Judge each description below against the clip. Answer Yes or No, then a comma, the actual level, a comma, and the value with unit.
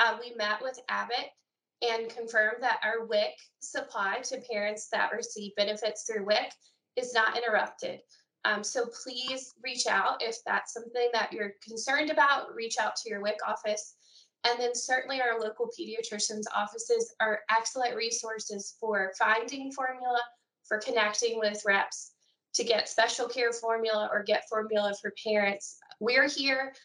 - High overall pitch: Yes, high, 225 Hz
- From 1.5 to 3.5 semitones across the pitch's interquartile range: Yes, average, 2.8 semitones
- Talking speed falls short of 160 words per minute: Yes, average, 150 wpm